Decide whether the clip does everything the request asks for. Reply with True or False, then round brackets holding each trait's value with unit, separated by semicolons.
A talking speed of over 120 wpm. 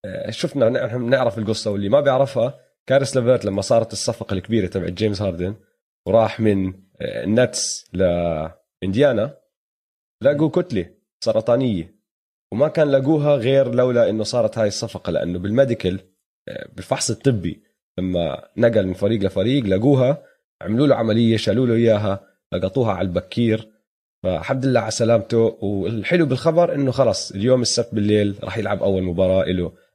True (135 wpm)